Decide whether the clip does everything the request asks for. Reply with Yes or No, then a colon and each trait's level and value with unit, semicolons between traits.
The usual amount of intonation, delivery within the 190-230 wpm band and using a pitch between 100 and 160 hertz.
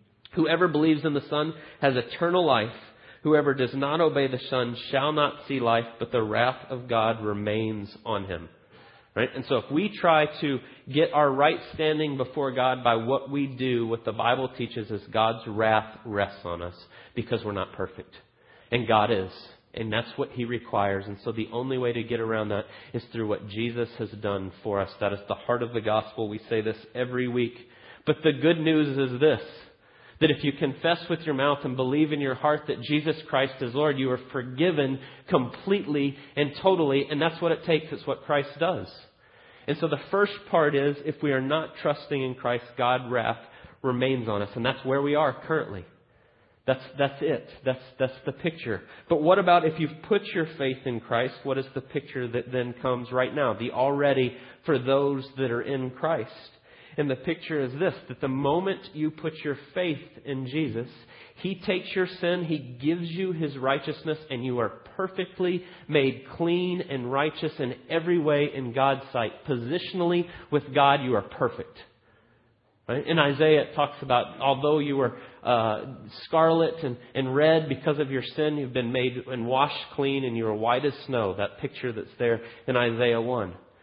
Yes: average, 4.2 semitones; average, 195 wpm; low, 135 Hz